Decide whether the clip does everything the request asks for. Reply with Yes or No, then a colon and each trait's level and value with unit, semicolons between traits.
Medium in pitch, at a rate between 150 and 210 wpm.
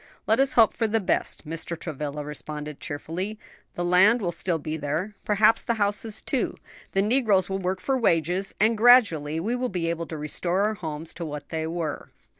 Yes: medium, 180 Hz; average, 195 wpm